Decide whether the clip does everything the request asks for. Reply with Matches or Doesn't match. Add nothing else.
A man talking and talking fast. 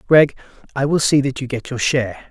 Matches